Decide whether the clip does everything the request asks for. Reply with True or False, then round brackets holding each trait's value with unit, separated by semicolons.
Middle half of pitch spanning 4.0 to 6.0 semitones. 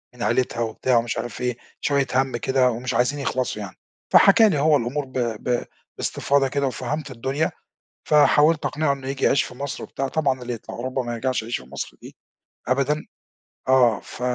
False (2.7 semitones)